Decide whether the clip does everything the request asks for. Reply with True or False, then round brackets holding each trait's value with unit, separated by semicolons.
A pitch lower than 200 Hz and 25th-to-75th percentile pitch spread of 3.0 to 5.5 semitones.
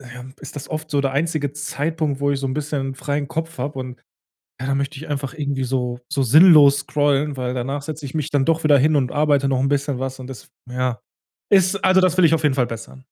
False (140 Hz; 2.4 semitones)